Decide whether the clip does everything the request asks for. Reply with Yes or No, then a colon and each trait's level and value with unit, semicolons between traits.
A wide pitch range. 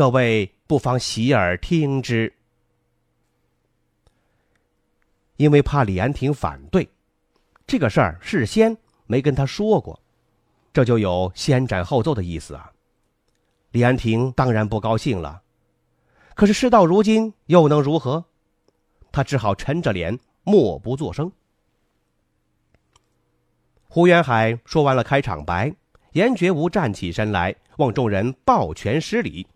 Yes: wide, 7.7 semitones